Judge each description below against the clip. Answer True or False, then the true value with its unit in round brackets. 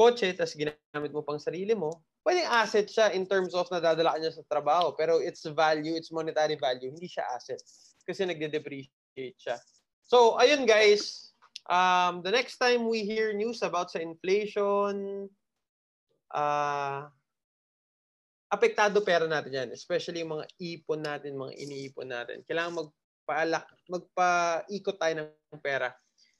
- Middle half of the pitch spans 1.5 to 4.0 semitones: False (4.6 semitones)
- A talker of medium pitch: True (170 Hz)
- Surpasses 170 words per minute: False (140 wpm)